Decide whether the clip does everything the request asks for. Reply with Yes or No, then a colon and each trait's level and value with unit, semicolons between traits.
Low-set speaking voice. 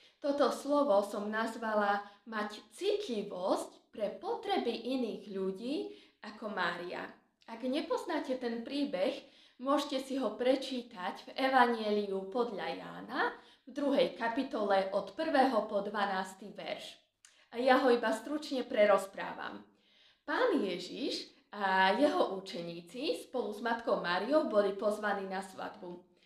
No: high, 235 Hz